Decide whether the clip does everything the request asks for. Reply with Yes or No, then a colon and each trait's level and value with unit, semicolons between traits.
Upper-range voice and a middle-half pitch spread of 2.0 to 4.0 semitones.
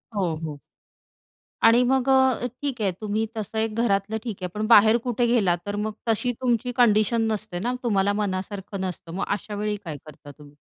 Yes: high, 210 Hz; average, 3.5 semitones